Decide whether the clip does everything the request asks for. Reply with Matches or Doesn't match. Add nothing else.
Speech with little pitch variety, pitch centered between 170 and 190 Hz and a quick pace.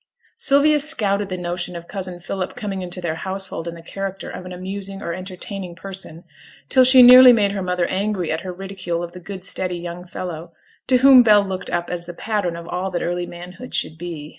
Matches